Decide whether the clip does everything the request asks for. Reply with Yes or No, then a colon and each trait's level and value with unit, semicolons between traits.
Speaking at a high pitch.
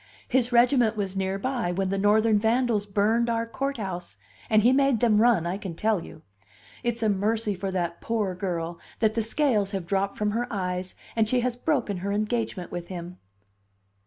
Yes: high, 210 Hz